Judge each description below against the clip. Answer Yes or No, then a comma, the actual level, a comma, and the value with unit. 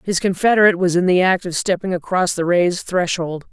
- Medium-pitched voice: Yes, medium, 180 Hz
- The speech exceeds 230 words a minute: No, fast, 205 wpm